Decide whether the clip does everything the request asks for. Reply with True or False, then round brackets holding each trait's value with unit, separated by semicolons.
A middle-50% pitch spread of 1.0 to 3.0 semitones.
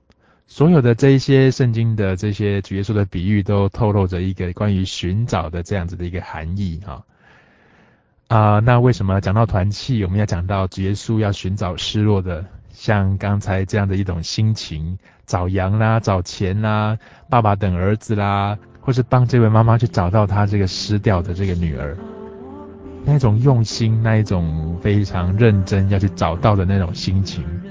True (2.7 semitones)